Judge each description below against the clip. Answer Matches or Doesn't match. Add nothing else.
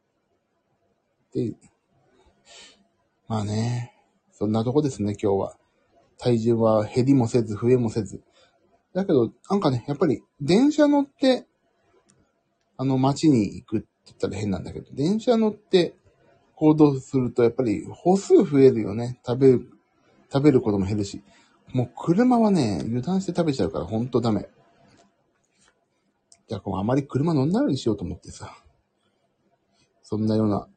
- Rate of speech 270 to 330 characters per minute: Matches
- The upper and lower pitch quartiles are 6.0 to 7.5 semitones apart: Matches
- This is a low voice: Matches